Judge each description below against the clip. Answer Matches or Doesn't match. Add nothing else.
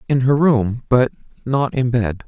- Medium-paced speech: Matches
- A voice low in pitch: Matches